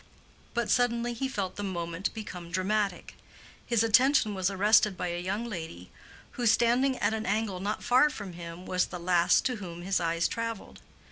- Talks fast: No, average, 180 wpm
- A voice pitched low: No, high, 200 Hz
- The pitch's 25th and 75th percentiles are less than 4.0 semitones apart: No, average, 4.4 semitones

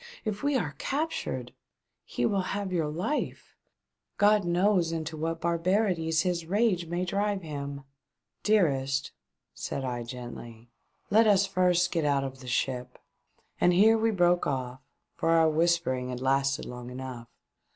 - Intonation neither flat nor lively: No, wide, 6.1 semitones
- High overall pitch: No, medium, 165 Hz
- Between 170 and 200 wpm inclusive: No, average, 160 wpm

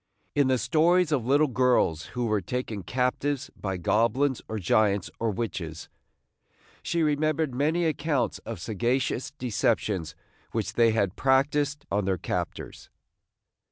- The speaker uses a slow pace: Yes, slow, 130 wpm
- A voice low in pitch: Yes, low, 125 Hz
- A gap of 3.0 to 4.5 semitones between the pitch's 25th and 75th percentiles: No, wide, 5.5 semitones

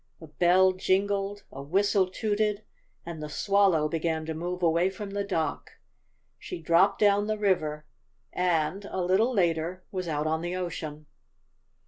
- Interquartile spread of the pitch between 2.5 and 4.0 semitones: Yes, average, 3.7 semitones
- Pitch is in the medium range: Yes, medium, 180 Hz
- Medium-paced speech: Yes, average, 150 wpm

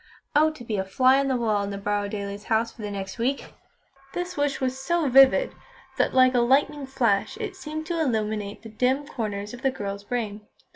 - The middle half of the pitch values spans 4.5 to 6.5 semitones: Yes, average, 5.0 semitones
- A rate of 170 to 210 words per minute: Yes, fast, 205 wpm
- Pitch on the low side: No, high, 245 Hz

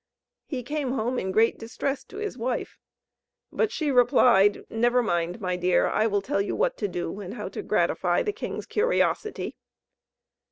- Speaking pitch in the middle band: No, high, 235 Hz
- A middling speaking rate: Yes, average, 170 wpm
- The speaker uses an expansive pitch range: Yes, wide, 5.9 semitones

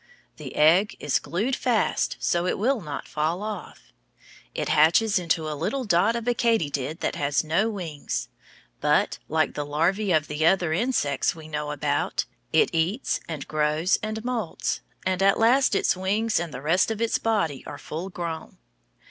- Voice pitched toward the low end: No, medium, 175 Hz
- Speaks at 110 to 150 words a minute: No, average, 175 wpm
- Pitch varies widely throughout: Yes, wide, 5.9 semitones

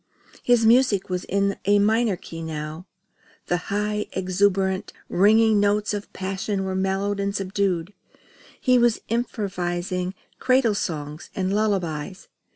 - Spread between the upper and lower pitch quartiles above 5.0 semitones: No, narrow, 2.4 semitones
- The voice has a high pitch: Yes, high, 195 Hz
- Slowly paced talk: Yes, slow, 125 wpm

